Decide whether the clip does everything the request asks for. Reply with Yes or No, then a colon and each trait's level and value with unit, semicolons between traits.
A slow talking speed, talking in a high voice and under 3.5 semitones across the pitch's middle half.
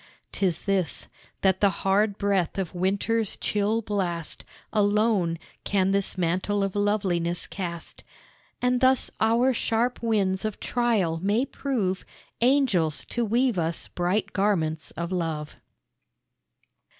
No: slow, 120 wpm; high, 200 Hz; average, 3.8 semitones